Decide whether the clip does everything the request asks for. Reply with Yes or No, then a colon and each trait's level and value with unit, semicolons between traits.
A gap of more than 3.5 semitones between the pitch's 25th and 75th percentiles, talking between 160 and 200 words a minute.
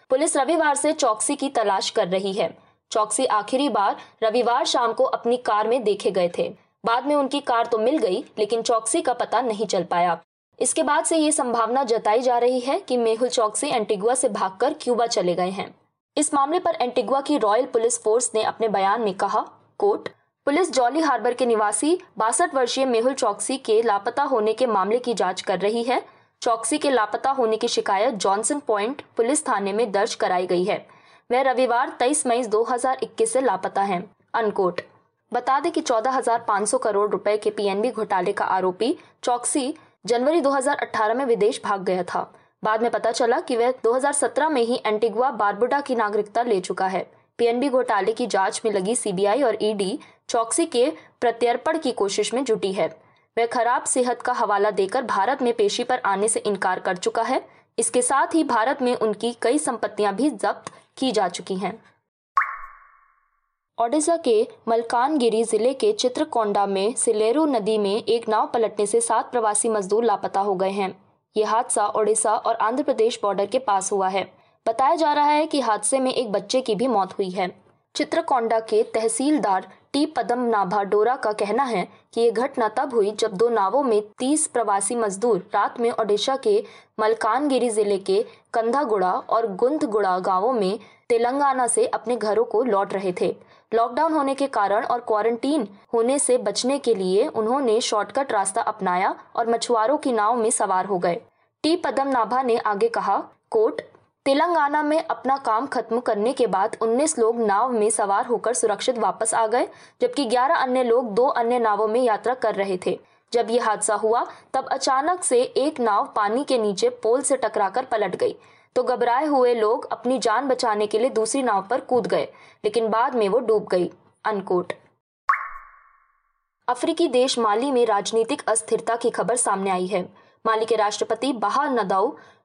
Yes: average, 4.0 semitones; average, 175 wpm